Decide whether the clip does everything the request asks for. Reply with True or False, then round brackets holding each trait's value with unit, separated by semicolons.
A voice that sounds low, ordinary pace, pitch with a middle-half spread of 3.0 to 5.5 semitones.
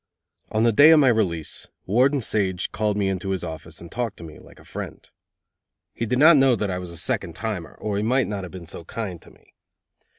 False (105 Hz; 235 wpm; 4.9 semitones)